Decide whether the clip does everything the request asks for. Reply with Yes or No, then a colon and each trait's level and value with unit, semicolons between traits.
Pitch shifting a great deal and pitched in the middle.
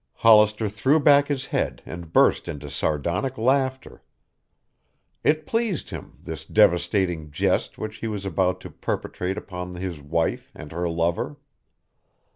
No: wide, 7.5 semitones; very low, 95 Hz